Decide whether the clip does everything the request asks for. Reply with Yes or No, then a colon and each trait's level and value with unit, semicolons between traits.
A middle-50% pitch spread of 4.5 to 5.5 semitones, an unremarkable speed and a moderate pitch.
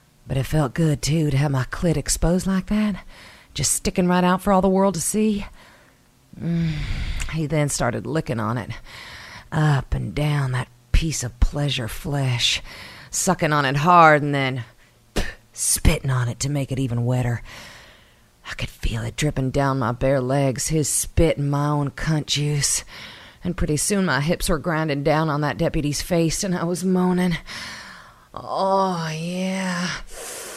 Yes: average, 5.0 semitones; average, 170 wpm; medium, 150 Hz